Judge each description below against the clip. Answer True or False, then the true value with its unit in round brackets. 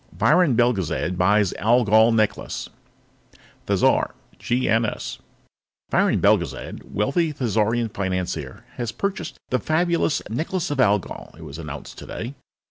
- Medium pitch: False (115 Hz)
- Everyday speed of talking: False (110 wpm)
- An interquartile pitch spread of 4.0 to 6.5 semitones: True (5.2 semitones)